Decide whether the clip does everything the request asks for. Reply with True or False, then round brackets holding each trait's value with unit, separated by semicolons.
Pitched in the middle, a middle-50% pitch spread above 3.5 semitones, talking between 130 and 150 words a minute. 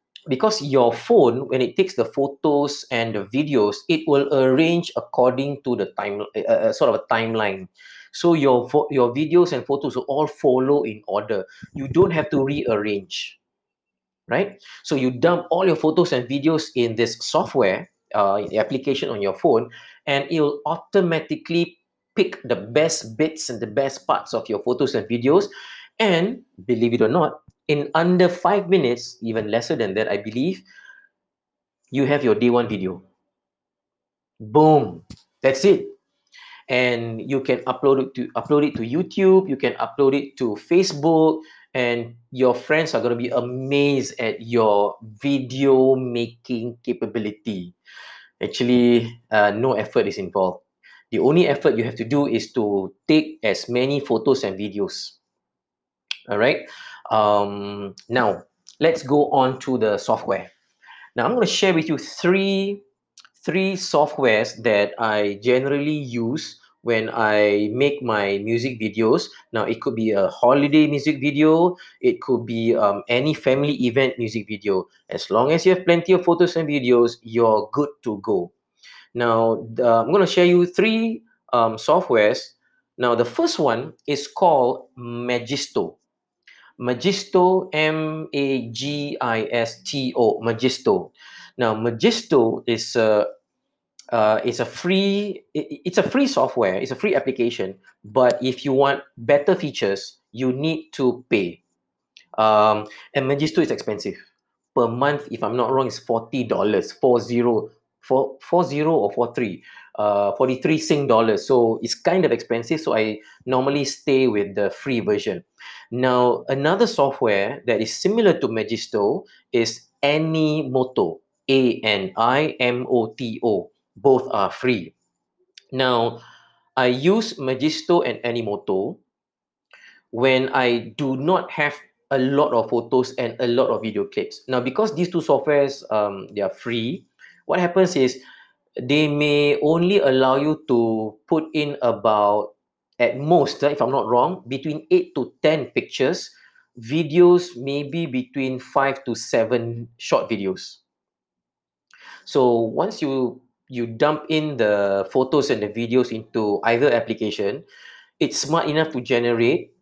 False (130 Hz; 4.9 semitones; 145 wpm)